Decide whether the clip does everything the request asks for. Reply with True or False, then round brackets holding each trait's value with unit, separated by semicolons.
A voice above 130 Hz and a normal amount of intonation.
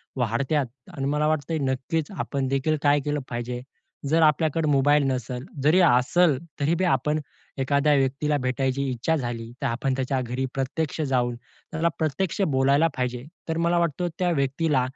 True (140 Hz; 3.2 semitones)